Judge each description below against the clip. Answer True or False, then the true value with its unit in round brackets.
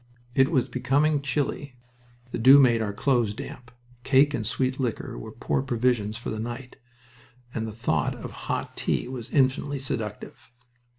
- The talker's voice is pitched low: True (125 Hz)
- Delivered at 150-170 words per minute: True (160 wpm)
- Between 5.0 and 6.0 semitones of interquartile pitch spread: False (3.1 semitones)